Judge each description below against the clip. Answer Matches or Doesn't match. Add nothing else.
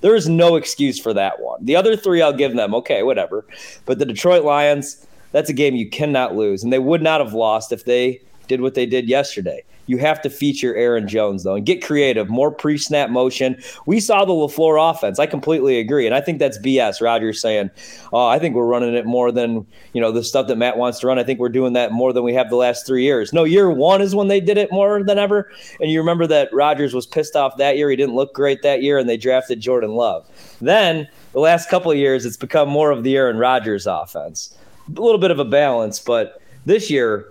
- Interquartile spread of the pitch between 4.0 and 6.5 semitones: Matches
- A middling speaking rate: Doesn't match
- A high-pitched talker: Doesn't match